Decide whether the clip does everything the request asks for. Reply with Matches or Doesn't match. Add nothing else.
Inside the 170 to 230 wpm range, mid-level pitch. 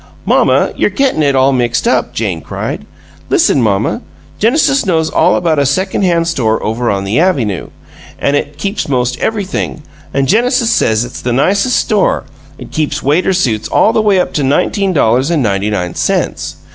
Matches